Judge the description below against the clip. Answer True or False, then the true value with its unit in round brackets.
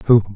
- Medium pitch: False (110 Hz)